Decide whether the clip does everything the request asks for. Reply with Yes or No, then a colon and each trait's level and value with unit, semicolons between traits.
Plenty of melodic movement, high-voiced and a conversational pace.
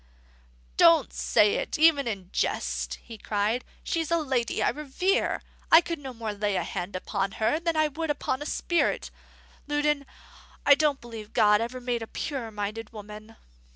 Yes: wide, 6.0 semitones; high, 240 Hz; average, 170 wpm